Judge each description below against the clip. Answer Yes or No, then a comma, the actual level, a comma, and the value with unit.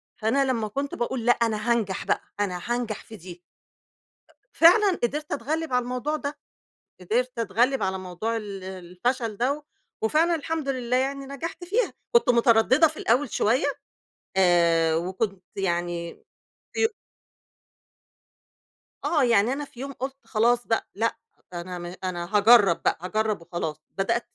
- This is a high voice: Yes, high, 230 Hz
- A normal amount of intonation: No, wide, 6.0 semitones